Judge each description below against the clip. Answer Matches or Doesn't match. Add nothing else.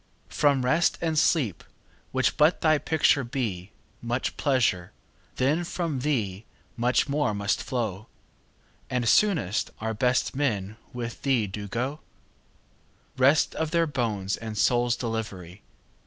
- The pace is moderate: Doesn't match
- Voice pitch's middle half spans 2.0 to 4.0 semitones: Doesn't match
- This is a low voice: Matches